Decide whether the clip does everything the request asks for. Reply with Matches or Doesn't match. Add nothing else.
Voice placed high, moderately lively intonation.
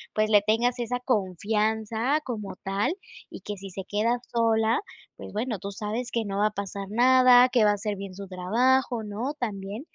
Matches